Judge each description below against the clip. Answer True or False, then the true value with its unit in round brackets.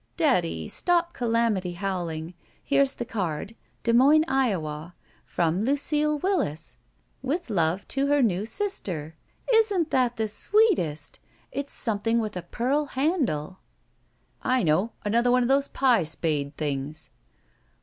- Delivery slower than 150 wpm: True (135 wpm)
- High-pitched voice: True (230 Hz)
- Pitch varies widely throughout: True (8.6 semitones)